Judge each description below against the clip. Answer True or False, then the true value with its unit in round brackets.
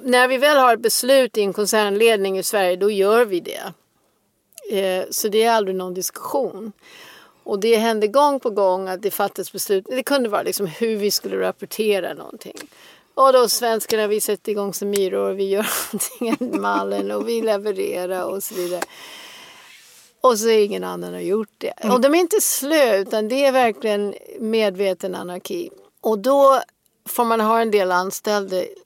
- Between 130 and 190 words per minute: True (180 wpm)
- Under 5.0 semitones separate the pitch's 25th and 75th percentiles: True (4.1 semitones)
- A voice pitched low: False (210 Hz)